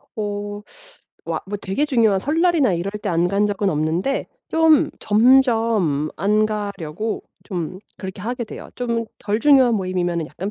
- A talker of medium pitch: No, high, 205 Hz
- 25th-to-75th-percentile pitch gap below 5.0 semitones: Yes, average, 4.3 semitones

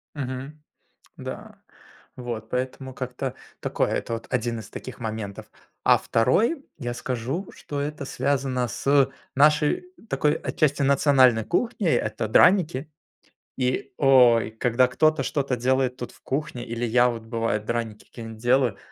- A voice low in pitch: Yes, low, 125 Hz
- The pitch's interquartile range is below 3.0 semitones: No, average, 3.3 semitones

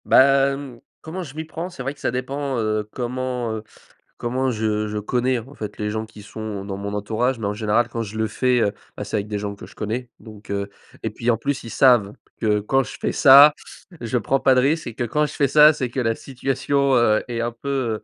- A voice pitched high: No, low, 120 Hz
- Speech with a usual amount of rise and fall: Yes, average, 3.9 semitones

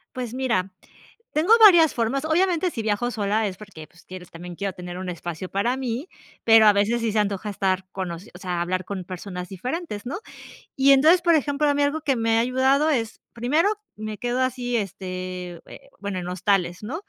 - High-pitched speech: Yes, high, 215 Hz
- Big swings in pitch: Yes, wide, 6.2 semitones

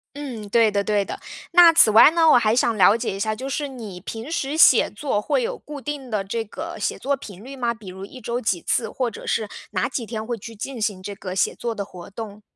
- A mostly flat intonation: No, average, 4.7 semitones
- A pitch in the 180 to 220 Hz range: No, high, 230 Hz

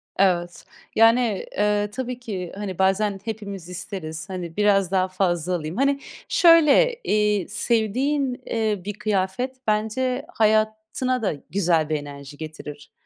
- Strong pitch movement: No, average, 3.9 semitones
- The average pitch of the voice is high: Yes, high, 205 Hz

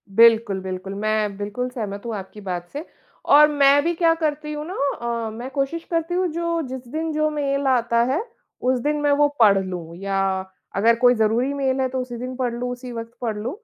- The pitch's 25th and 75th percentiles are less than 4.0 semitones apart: No, average, 5.3 semitones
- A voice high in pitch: Yes, very high, 250 Hz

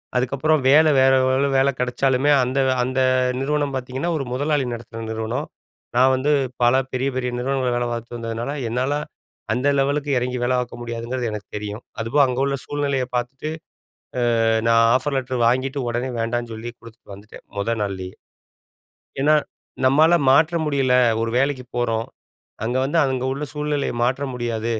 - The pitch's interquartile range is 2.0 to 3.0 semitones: Yes, average, 2.7 semitones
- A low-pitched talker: Yes, low, 130 Hz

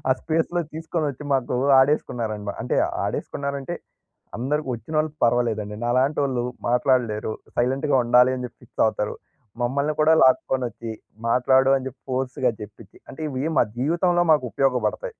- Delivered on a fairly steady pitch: No, average, 3.4 semitones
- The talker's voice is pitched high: No, low, 130 Hz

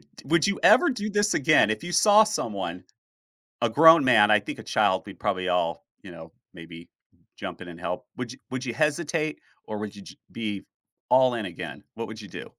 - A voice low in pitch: Yes, low, 120 Hz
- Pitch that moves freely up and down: Yes, wide, 8.3 semitones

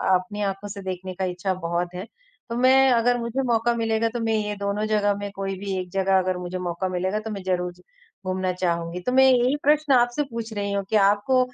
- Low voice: No, high, 200 Hz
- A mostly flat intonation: No, average, 3.8 semitones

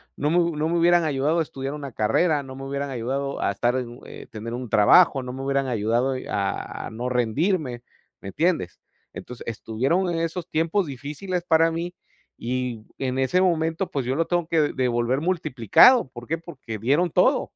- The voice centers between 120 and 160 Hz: Yes, medium, 140 Hz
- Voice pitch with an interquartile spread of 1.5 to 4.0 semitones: No, average, 5.2 semitones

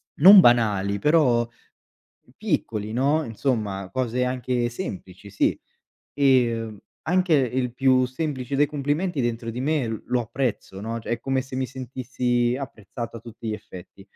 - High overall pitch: No, low, 125 Hz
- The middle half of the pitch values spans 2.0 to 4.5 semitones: Yes, average, 2.8 semitones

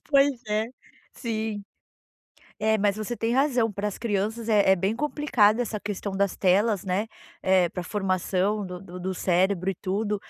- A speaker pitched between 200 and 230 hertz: Yes, high, 205 Hz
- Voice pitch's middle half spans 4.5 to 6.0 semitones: No, average, 2.7 semitones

